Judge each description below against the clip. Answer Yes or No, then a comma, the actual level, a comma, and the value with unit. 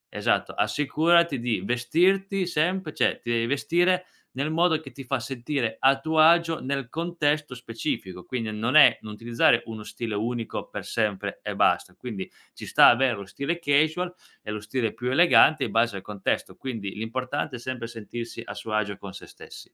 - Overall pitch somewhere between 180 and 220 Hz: No, low, 130 Hz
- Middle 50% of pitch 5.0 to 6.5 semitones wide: Yes, wide, 5.5 semitones